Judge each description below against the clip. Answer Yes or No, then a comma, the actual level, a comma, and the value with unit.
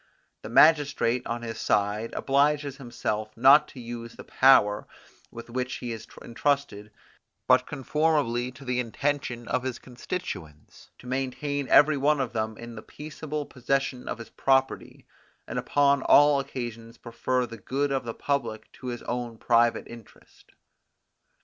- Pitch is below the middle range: Yes, low, 125 Hz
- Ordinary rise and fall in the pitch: Yes, average, 3.3 semitones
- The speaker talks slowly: No, average, 150 wpm